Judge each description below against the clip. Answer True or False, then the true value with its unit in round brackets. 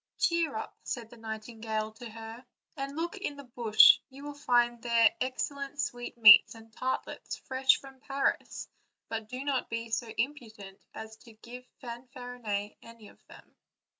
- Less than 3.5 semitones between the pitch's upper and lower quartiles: True (3.1 semitones)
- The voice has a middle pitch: False (240 Hz)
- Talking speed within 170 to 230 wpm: False (160 wpm)